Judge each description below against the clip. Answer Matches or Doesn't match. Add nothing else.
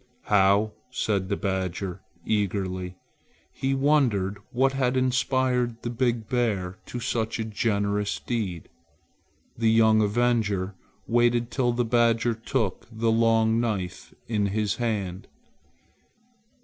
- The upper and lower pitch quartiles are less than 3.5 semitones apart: Matches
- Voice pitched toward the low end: Matches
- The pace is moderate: Doesn't match